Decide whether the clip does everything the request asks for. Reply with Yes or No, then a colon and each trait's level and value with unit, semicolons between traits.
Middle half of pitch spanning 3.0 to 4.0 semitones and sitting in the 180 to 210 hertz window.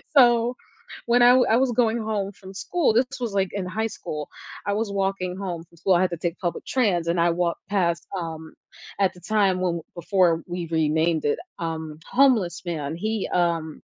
No: average, 4.5 semitones; medium, 185 Hz